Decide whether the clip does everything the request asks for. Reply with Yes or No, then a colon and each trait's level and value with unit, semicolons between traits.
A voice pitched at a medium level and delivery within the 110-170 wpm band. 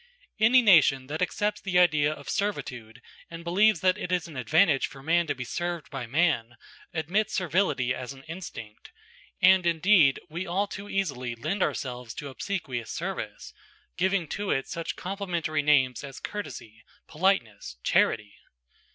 Yes: medium, 160 Hz; average, 150 wpm